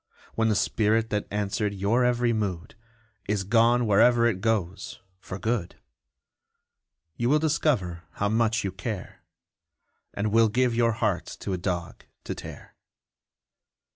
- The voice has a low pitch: Yes, low, 110 Hz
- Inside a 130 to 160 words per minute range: Yes, average, 140 wpm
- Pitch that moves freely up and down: No, average, 3.1 semitones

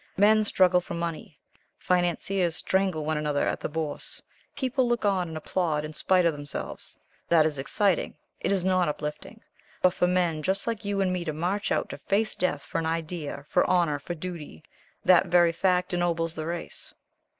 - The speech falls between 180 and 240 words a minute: Yes, average, 185 wpm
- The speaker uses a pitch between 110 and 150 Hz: No, medium, 175 Hz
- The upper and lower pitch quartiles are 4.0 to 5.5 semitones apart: No, average, 3.1 semitones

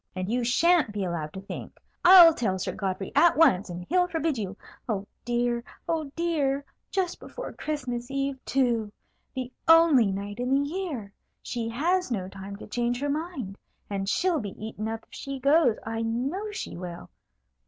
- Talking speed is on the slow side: No, average, 175 wpm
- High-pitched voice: Yes, high, 245 Hz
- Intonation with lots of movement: Yes, wide, 7.3 semitones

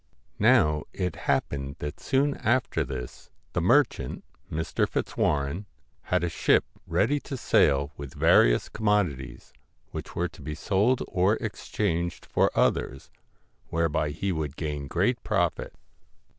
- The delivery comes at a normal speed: No, slow, 130 wpm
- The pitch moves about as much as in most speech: No, wide, 6.3 semitones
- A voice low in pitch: Yes, very low, 80 Hz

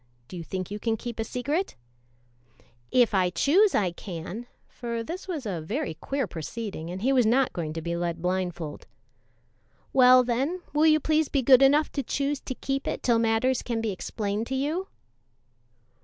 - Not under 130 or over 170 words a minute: No, average, 185 wpm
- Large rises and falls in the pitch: Yes, wide, 6.6 semitones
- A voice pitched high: Yes, high, 235 Hz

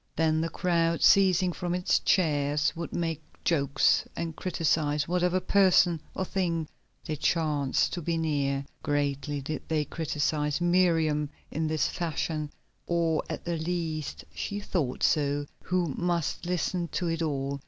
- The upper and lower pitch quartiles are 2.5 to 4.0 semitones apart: Yes, average, 2.8 semitones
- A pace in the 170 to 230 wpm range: No, average, 145 wpm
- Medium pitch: Yes, medium, 160 Hz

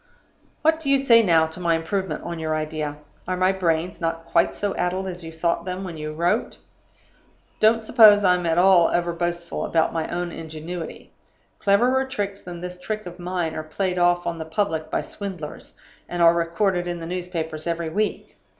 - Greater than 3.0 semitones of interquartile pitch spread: No, average, 2.7 semitones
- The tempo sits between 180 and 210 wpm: Yes, average, 185 wpm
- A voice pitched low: No, medium, 175 Hz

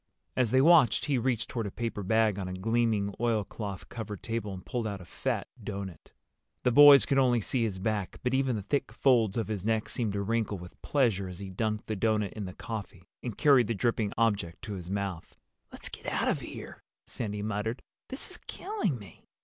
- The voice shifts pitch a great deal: No, average, 3.2 semitones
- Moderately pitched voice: No, low, 110 Hz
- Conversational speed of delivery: No, fast, 210 wpm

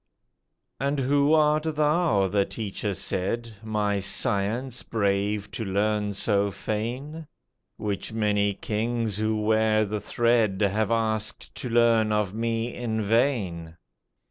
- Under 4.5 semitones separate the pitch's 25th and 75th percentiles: Yes, narrow, 2.5 semitones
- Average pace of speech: No, slow, 120 wpm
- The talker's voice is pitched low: Yes, low, 110 Hz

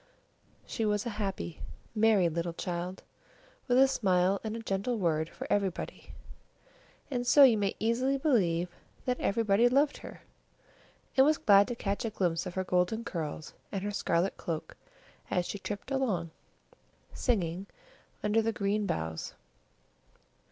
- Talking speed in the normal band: Yes, average, 145 wpm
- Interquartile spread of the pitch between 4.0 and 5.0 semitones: Yes, average, 4.5 semitones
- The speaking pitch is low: No, high, 200 Hz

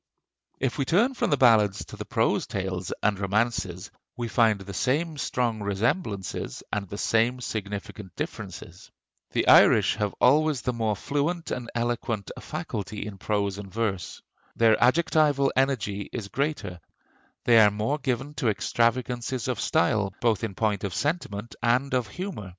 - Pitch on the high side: No, low, 115 Hz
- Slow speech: No, average, 155 wpm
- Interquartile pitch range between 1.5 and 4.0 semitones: No, average, 4.5 semitones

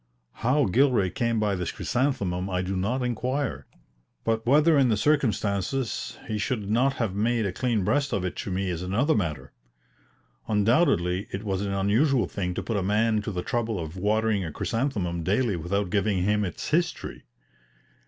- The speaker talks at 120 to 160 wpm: No, average, 175 wpm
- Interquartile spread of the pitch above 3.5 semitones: Yes, average, 4.6 semitones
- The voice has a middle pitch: No, low, 105 Hz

